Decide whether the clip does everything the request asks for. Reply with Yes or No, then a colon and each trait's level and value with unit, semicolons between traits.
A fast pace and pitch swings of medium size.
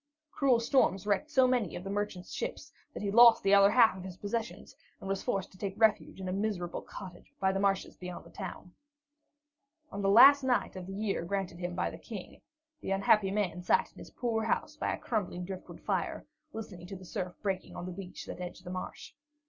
Yes: fast, 220 wpm; average, 3.0 semitones